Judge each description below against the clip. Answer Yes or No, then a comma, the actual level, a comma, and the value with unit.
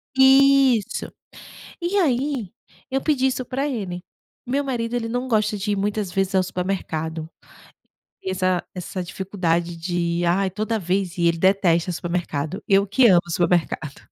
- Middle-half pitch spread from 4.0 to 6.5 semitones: Yes, wide, 5.5 semitones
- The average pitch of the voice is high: Yes, high, 195 Hz